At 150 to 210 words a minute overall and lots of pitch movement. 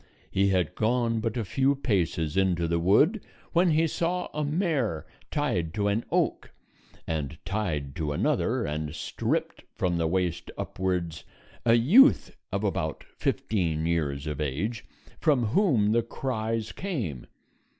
No: average, 140 wpm; wide, 8.1 semitones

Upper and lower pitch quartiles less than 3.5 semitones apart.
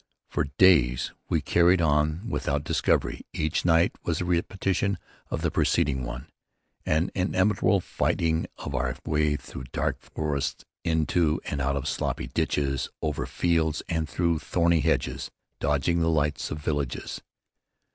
Yes: average, 2.9 semitones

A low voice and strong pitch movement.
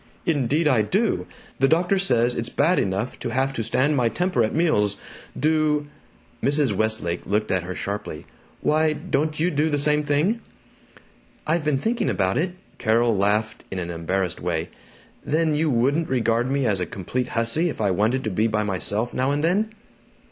Yes: low, 130 Hz; wide, 6.4 semitones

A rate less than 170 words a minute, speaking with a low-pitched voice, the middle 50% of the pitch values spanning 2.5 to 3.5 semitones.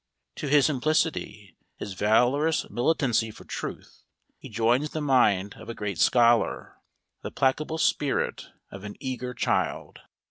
No: slow, 135 wpm; low, 125 Hz; average, 5.1 semitones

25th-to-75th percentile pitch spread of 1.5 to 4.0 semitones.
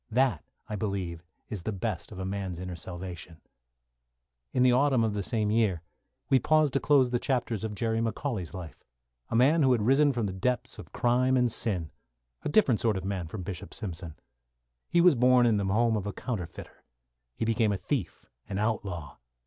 No: average, 4.8 semitones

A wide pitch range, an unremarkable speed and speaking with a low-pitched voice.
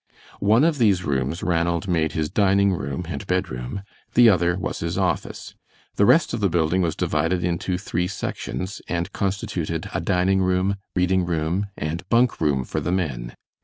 No: average, 3.1 semitones; average, 170 wpm; very low, 90 Hz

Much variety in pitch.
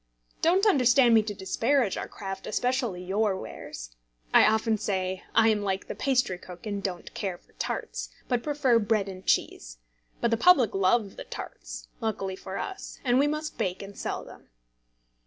No: average, 4.5 semitones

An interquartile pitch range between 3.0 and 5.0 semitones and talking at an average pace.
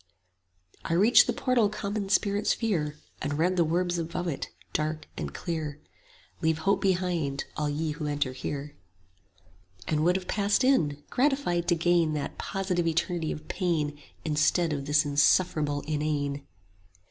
Yes: average, 3.7 semitones; average, 150 wpm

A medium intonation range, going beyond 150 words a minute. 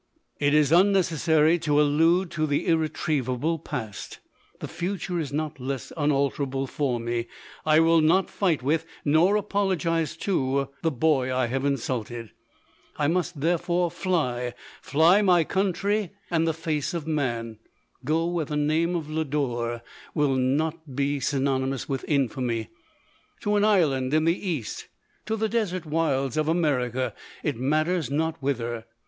Yes: average, 4.0 semitones; average, 160 wpm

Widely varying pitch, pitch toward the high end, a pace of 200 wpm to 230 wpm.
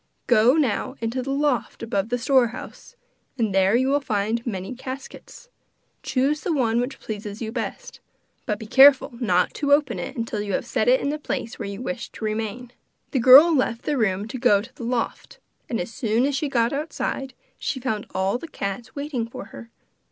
No: average, 3.9 semitones; high, 245 Hz; fast, 205 wpm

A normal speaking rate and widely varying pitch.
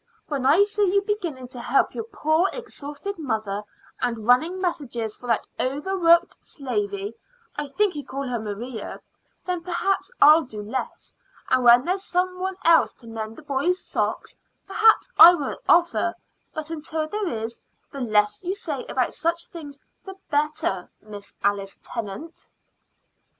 Yes: average, 155 wpm; wide, 6.9 semitones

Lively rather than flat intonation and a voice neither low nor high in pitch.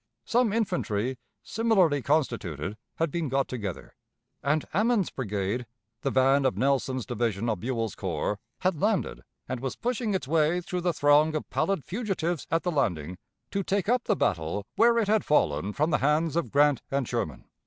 Yes: wide, 7.3 semitones; medium, 145 Hz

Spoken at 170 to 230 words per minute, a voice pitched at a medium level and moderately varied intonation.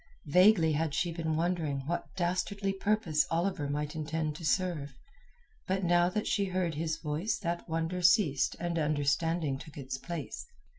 No: average, 155 wpm; medium, 165 Hz; average, 3.2 semitones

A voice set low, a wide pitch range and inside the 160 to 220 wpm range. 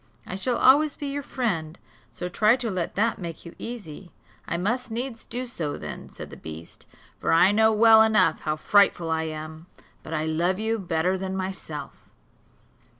No: high, 190 Hz; wide, 5.8 semitones; average, 180 wpm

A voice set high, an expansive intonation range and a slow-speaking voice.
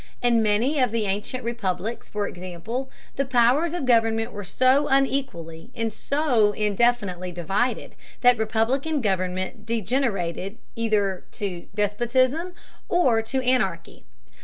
No: high, 225 Hz; average, 4.6 semitones; slow, 120 wpm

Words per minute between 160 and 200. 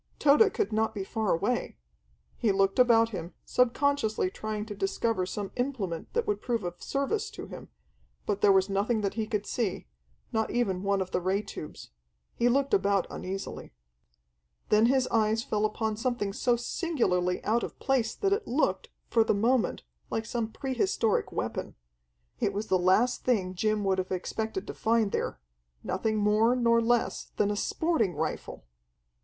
Yes: average, 170 wpm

